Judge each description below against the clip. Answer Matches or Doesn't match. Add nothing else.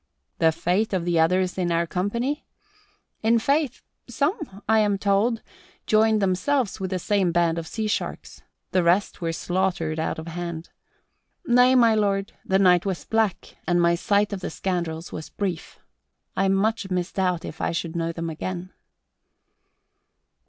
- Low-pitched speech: Doesn't match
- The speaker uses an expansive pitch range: Doesn't match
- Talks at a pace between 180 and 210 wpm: Doesn't match